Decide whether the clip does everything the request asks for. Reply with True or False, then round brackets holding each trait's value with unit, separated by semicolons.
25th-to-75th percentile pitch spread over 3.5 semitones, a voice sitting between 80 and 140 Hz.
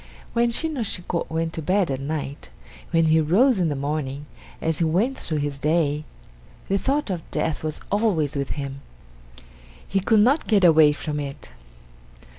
False (5.2 semitones; 160 Hz)